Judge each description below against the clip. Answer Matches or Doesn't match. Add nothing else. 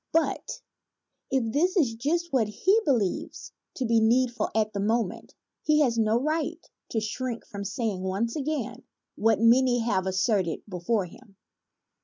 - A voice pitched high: Matches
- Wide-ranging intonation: Doesn't match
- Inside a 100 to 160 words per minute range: Matches